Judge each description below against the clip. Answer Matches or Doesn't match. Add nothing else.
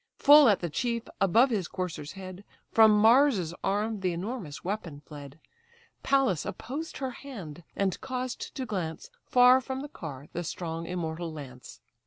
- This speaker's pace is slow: Doesn't match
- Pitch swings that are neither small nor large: Doesn't match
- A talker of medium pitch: Doesn't match